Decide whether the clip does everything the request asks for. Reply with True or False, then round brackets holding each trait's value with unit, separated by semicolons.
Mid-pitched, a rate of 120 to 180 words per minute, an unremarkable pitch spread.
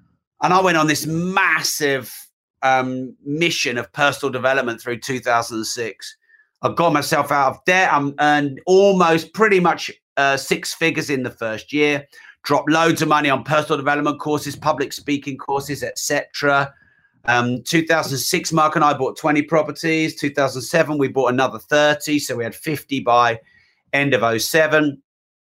True (145 Hz; 175 wpm; 3.1 semitones)